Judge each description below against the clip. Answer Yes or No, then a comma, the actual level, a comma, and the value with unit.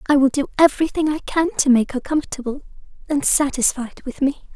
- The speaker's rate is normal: Yes, average, 185 wpm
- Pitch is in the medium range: No, very high, 275 Hz